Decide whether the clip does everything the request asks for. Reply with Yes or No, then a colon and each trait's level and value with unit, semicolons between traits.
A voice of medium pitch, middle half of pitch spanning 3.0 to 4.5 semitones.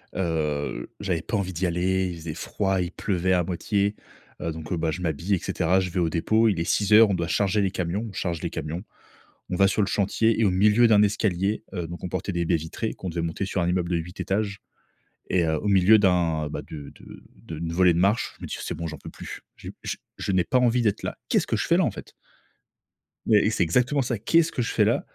No: very low, 95 Hz; average, 3.5 semitones